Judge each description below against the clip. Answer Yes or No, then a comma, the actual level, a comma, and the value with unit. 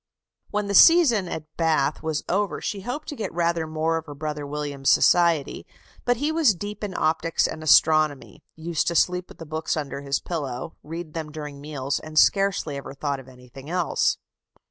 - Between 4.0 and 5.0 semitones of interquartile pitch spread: No, average, 3.5 semitones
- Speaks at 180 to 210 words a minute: Yes, average, 190 wpm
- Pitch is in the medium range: Yes, medium, 160 Hz